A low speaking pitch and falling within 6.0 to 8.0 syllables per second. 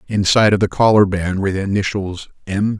Yes: low, 100 Hz; 6.1 syllables/s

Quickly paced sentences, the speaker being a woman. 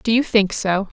Yes: fast, 240 wpm; female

